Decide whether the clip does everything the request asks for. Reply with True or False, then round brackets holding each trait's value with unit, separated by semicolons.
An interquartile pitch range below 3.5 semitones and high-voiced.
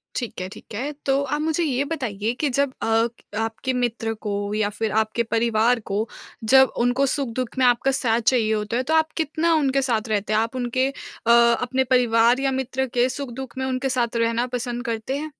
True (2.9 semitones; 245 Hz)